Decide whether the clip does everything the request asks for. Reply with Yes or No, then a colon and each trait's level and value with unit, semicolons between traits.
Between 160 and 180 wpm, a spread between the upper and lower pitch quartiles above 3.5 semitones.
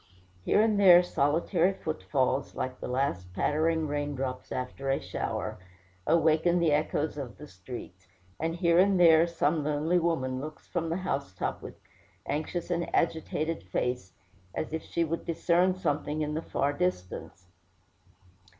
No: average, 150 wpm; average, 3.9 semitones